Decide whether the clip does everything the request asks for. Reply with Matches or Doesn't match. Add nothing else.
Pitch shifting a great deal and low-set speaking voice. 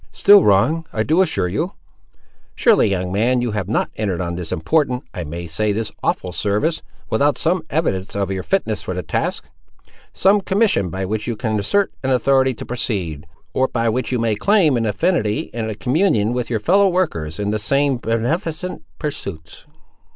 Matches